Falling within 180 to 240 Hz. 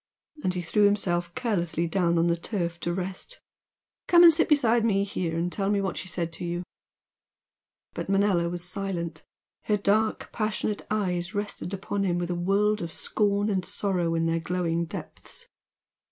Yes: medium, 185 Hz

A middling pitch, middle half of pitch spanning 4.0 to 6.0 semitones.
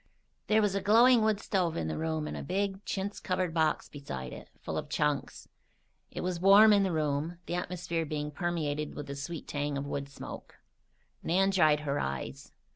Yes: medium, 165 Hz; average, 4.7 semitones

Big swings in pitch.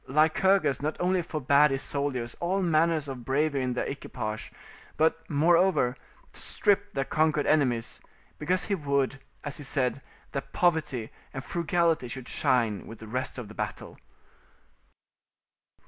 No: average, 4.4 semitones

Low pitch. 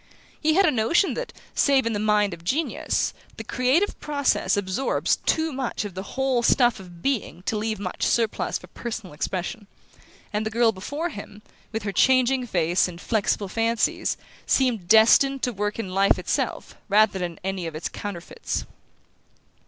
No: high, 220 Hz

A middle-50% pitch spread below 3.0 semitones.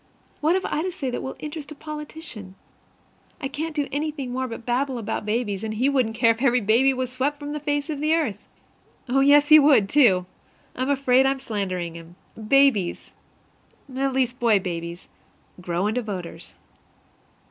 No: average, 5.2 semitones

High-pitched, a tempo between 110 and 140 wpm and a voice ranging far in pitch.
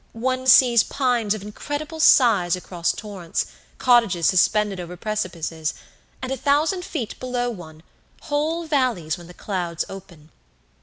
Yes: high, 215 Hz; slow, 135 wpm; wide, 6.7 semitones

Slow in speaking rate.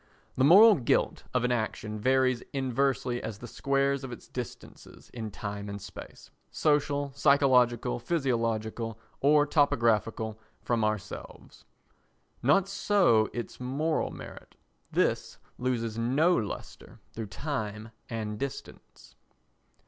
Yes: slow, 115 wpm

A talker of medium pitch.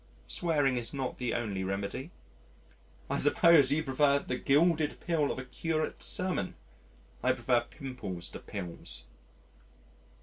No: low, 130 Hz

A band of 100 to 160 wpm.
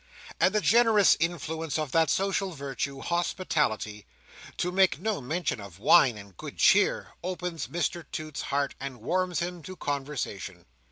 Yes: average, 150 wpm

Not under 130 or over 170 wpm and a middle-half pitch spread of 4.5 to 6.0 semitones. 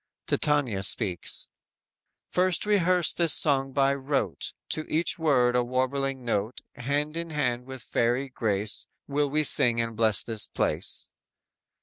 No: average, 140 wpm; average, 4.1 semitones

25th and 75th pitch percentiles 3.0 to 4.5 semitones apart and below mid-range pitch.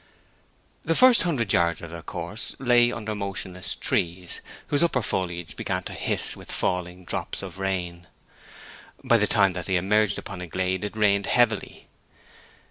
Yes: average, 3.7 semitones; very low, 95 Hz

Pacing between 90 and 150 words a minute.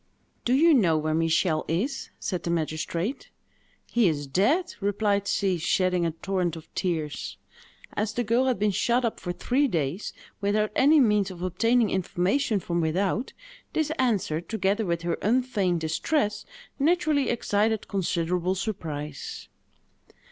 Yes: average, 140 wpm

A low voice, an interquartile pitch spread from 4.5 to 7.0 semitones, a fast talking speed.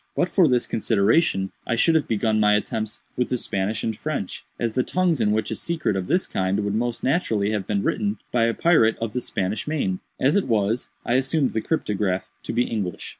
Yes: low, 115 Hz; average, 4.9 semitones; fast, 220 wpm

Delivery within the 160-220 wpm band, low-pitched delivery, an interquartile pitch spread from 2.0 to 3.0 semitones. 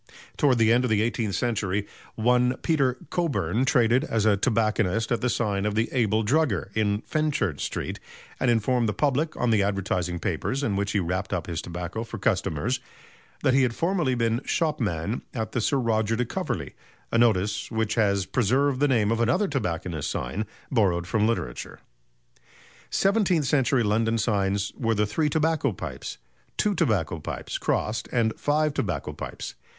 No: average, 170 wpm; low, 115 Hz; average, 4.0 semitones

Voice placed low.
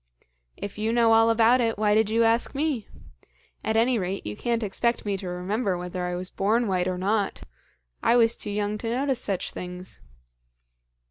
No: high, 215 Hz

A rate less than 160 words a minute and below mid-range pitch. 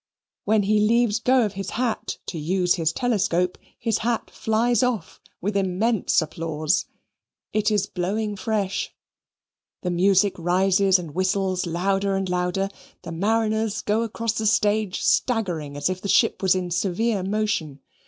No: average, 150 wpm; high, 195 Hz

